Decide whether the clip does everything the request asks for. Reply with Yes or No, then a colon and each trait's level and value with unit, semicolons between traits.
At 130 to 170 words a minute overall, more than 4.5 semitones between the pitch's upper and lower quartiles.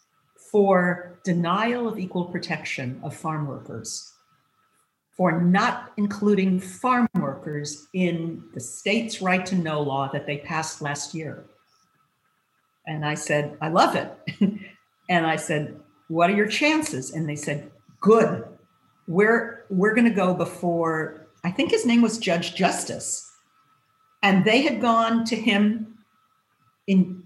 Yes: slow, 135 wpm; wide, 5.5 semitones